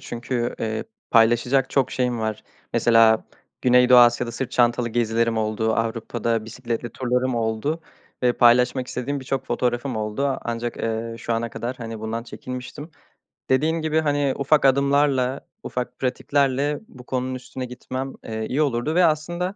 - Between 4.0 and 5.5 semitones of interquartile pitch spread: No, narrow, 2.6 semitones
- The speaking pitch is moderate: No, low, 125 Hz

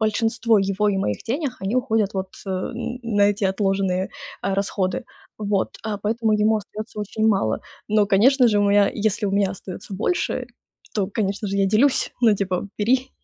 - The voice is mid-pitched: No, high, 205 Hz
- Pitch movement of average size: No, narrow, 2.3 semitones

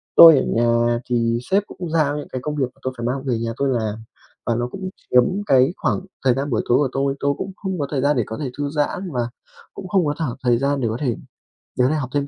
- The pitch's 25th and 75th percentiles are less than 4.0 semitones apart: Yes, average, 3.6 semitones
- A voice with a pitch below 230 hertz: Yes, low, 135 Hz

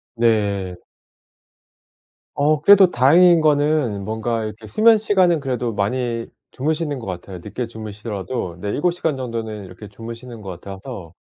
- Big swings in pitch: Yes, wide, 6.2 semitones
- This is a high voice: No, low, 115 Hz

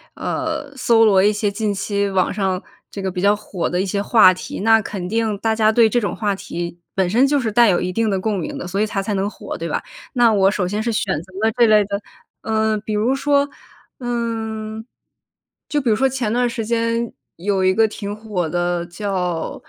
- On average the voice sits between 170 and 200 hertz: No, high, 210 Hz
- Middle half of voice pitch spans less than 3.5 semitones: Yes, average, 2.9 semitones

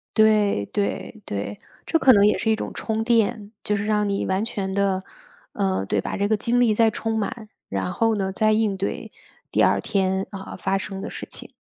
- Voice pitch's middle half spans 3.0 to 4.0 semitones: No, narrow, 2.4 semitones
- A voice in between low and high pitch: No, high, 205 Hz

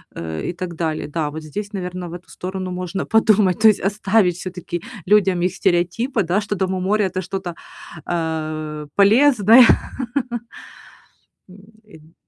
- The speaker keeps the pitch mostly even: No, average, 3.2 semitones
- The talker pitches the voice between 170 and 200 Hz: Yes, medium, 185 Hz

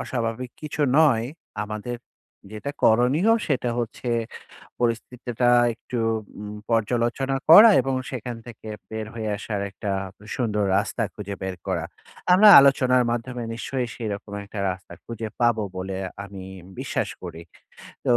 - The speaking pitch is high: No, low, 115 Hz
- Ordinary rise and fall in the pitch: Yes, average, 3.1 semitones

